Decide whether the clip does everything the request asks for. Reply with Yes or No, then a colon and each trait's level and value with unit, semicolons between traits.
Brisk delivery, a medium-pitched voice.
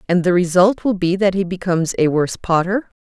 Yes: fast, 220 wpm; medium, 180 Hz